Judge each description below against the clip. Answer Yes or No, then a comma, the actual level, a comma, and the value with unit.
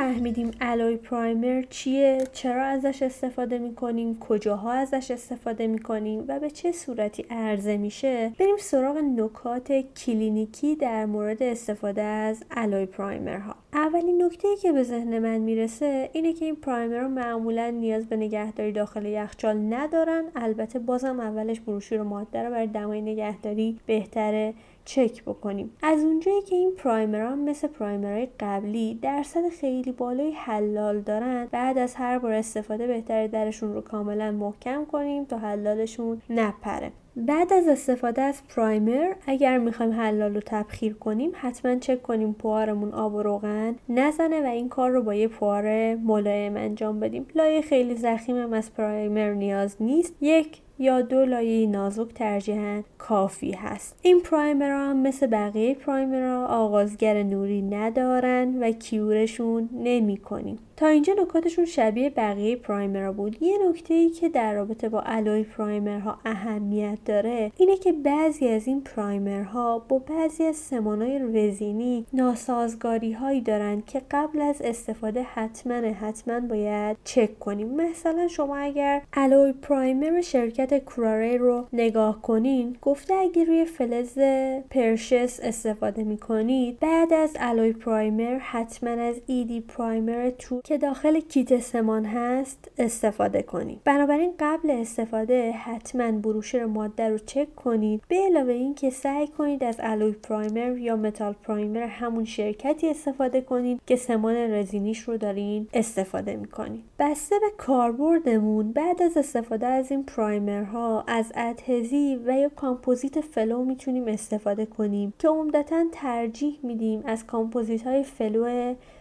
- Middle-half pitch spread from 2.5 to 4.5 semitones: Yes, average, 3.9 semitones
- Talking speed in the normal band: Yes, average, 145 wpm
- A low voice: No, high, 235 Hz